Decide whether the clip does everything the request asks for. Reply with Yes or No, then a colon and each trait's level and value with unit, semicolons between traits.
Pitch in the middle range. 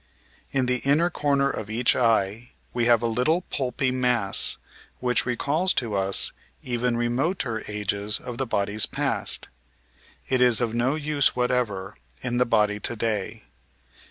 No: low, 120 Hz